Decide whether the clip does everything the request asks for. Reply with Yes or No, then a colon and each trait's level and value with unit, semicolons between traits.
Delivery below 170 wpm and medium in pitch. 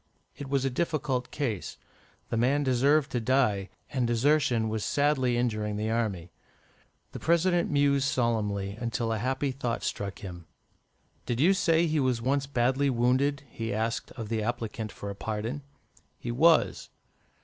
No: average, 160 wpm; low, 125 Hz